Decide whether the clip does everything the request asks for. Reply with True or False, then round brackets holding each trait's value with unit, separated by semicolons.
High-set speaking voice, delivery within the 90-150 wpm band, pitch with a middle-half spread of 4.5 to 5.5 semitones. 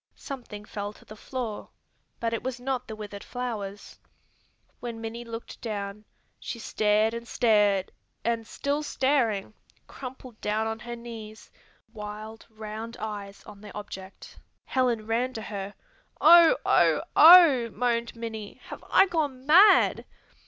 False (225 Hz; 140 wpm; 3.0 semitones)